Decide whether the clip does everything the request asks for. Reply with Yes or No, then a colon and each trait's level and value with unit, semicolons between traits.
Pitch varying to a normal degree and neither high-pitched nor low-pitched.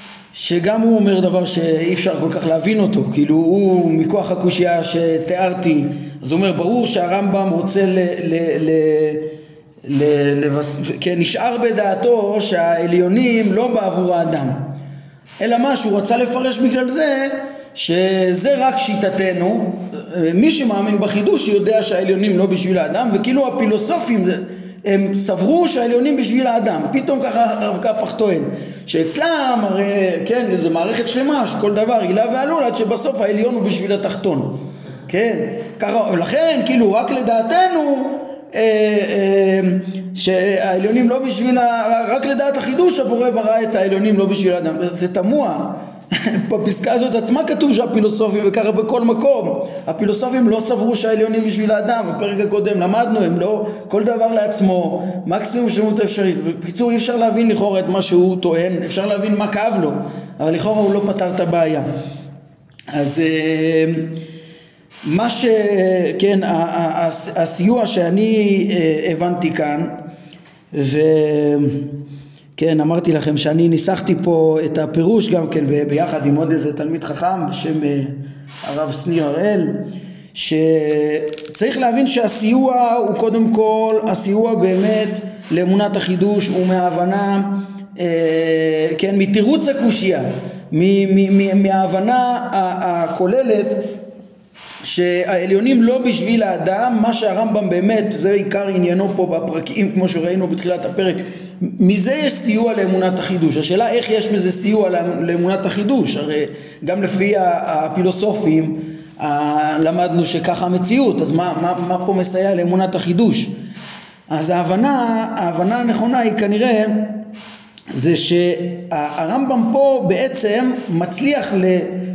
No: average, 4.7 semitones; high, 195 Hz